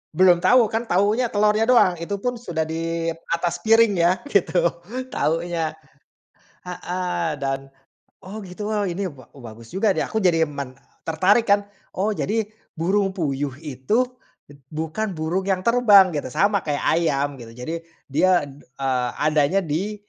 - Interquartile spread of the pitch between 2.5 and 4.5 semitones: No, average, 5.1 semitones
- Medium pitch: Yes, medium, 175 Hz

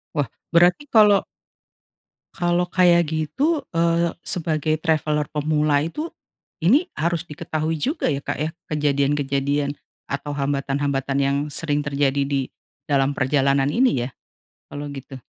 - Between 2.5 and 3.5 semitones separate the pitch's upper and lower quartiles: Yes, average, 3.2 semitones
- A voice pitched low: No, medium, 150 Hz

